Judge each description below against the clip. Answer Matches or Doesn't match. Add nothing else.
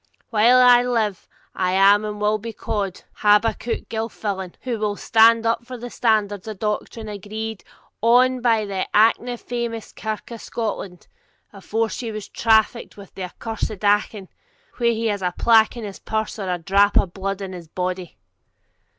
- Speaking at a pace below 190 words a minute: Matches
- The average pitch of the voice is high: Matches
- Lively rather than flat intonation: Doesn't match